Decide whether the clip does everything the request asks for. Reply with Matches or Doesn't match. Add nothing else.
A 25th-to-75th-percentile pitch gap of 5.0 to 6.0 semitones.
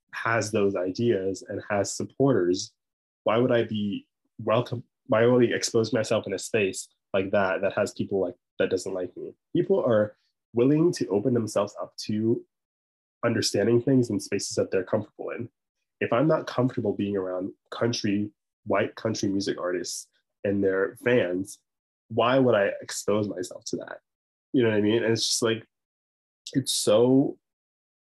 Doesn't match